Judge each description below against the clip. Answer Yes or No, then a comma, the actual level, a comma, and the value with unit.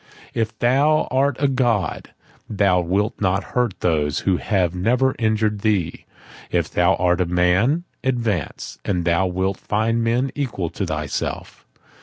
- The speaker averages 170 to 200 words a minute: No, average, 140 wpm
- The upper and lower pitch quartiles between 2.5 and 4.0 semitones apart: No, average, 5.0 semitones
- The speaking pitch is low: Yes, low, 105 Hz